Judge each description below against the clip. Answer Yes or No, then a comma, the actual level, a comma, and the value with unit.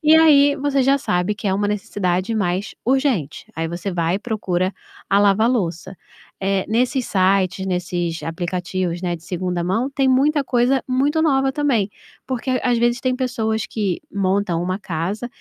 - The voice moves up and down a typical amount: No, wide, 6.1 semitones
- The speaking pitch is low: No, high, 205 Hz